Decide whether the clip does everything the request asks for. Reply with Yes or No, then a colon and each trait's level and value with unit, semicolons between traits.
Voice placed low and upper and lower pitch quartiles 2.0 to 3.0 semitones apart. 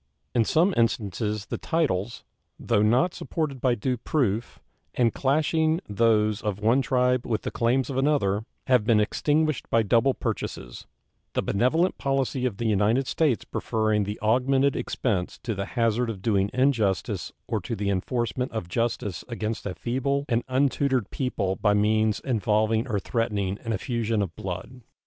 No: low, 115 Hz; average, 3.8 semitones